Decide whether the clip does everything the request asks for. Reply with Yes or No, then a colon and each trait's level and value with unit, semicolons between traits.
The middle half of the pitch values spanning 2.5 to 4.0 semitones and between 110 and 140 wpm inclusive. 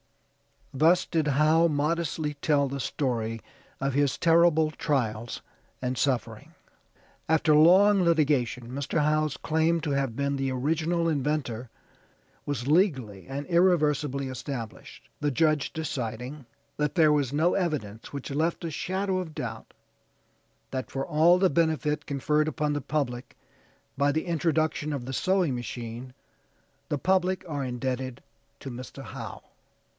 Yes: average, 3.5 semitones; slow, 135 wpm